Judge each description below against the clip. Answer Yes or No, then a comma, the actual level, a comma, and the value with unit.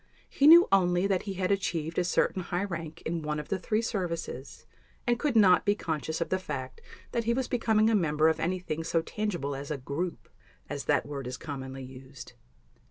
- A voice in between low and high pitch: Yes, medium, 170 Hz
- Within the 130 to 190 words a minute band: No, fast, 205 wpm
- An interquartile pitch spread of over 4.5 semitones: Yes, average, 5.0 semitones